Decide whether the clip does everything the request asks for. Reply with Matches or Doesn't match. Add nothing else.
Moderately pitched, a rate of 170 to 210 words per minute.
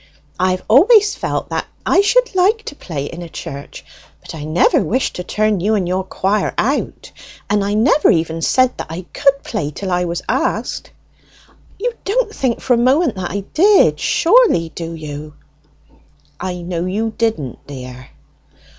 Doesn't match